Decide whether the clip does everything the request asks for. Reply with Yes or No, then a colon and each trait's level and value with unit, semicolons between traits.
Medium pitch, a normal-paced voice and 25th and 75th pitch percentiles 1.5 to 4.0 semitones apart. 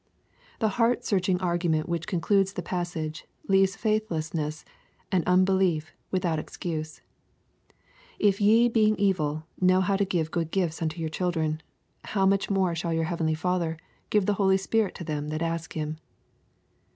Yes: medium, 180 Hz; average, 165 wpm; average, 3.3 semitones